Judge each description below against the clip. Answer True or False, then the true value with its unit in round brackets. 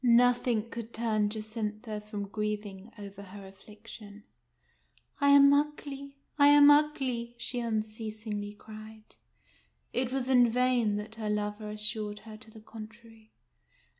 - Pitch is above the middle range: True (220 Hz)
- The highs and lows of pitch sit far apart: False (2.6 semitones)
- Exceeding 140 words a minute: False (135 wpm)